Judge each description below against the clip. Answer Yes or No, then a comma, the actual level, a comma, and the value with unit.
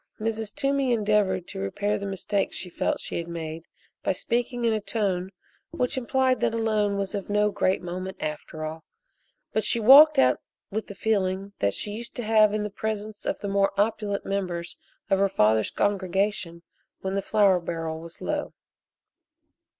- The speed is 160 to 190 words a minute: Yes, average, 180 wpm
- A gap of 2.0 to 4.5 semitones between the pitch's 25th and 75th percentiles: Yes, average, 3.1 semitones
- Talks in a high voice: Yes, high, 200 Hz